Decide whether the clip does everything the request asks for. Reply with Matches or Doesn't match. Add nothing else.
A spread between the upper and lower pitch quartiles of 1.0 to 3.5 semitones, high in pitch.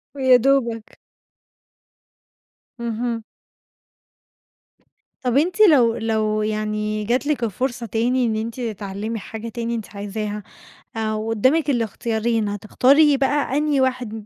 Matches